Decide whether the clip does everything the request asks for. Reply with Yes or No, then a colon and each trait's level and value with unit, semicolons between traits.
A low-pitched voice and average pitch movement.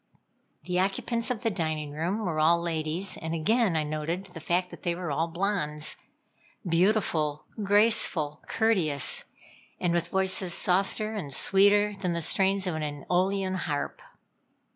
No: medium, 180 Hz; average, 3.9 semitones